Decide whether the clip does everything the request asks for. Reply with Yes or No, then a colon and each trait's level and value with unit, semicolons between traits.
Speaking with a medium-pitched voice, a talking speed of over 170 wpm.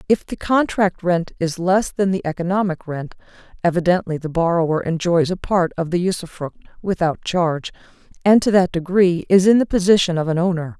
Yes: medium, 180 Hz; average, 180 wpm